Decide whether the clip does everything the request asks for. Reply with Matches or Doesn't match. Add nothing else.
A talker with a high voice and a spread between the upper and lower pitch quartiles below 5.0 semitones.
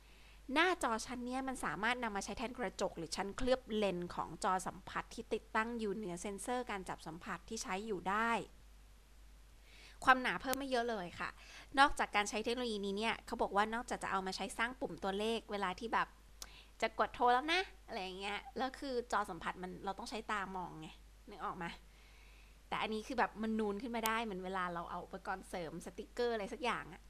Matches